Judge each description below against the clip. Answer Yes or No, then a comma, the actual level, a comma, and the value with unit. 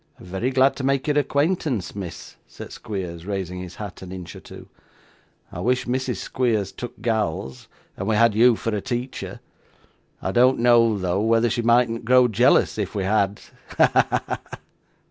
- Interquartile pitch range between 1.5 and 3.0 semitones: No, average, 4.2 semitones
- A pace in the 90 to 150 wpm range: No, average, 175 wpm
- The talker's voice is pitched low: Yes, low, 115 Hz